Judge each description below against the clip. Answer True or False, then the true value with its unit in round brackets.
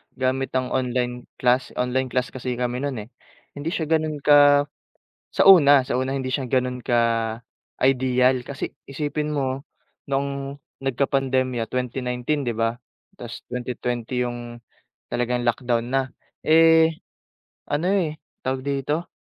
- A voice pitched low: True (130 Hz)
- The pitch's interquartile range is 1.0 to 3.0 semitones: True (2.4 semitones)